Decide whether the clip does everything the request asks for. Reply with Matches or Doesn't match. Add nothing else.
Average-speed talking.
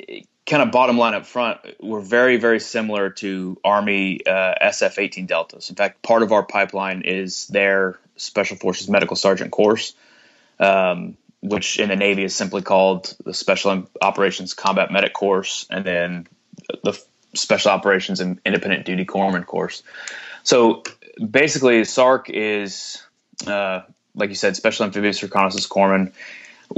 Matches